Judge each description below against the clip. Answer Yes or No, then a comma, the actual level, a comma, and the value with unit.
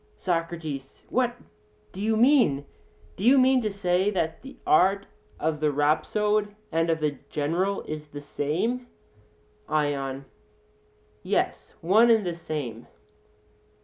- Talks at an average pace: No, slow, 125 wpm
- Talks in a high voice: No, medium, 170 Hz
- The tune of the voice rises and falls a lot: Yes, wide, 6.0 semitones